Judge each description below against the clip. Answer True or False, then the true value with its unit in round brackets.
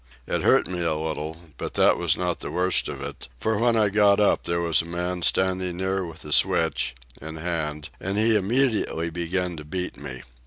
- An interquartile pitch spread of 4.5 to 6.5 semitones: False (3.0 semitones)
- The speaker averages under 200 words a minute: False (205 wpm)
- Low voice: True (90 Hz)